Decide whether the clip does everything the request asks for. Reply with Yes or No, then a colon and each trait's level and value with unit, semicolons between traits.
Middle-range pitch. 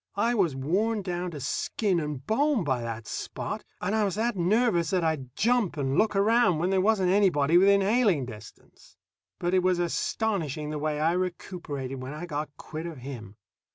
Yes: medium, 175 Hz